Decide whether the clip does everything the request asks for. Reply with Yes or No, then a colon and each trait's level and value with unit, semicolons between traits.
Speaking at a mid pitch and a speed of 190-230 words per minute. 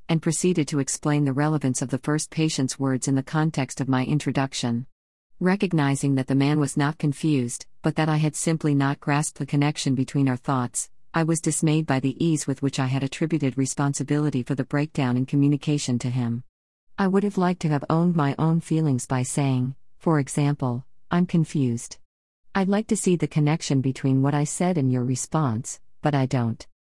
Yes: medium, 145 Hz; average, 195 wpm